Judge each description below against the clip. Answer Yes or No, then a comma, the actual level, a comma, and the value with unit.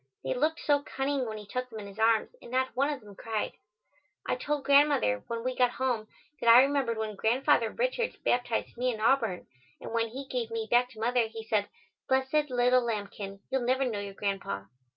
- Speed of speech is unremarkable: No, fast, 210 wpm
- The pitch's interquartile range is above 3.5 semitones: No, average, 3.2 semitones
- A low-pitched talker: No, high, 240 Hz